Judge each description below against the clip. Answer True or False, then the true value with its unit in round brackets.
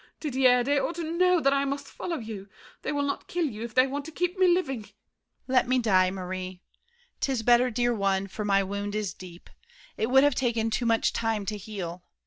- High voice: True (240 Hz)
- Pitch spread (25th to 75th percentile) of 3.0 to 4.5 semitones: False (5.6 semitones)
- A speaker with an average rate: False (220 wpm)